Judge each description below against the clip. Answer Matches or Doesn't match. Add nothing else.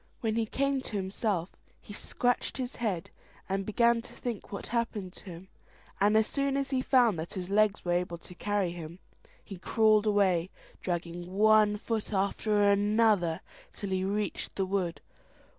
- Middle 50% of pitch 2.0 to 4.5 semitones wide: Matches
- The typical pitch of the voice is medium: Doesn't match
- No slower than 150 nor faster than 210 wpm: Matches